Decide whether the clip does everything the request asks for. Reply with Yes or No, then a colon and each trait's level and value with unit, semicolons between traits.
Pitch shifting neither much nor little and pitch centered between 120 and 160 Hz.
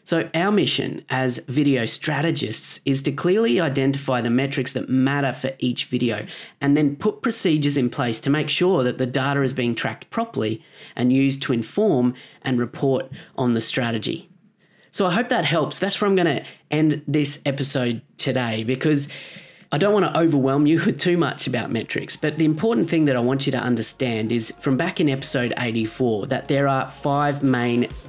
Yes: average, 4.0 semitones; medium, 140 Hz